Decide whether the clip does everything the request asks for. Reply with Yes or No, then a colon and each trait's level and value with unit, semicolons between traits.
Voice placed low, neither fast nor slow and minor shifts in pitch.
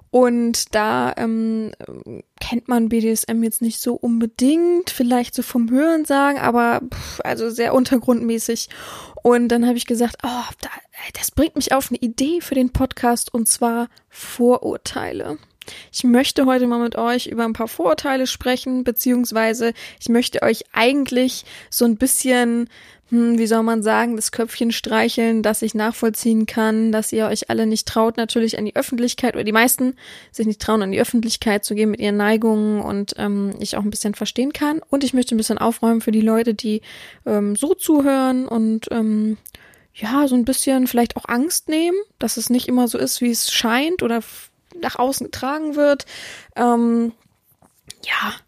No: high, 235 Hz; average, 170 wpm; narrow, 2.2 semitones